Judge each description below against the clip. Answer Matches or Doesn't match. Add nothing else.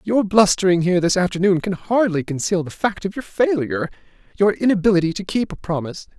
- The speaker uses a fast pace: Doesn't match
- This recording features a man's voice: Matches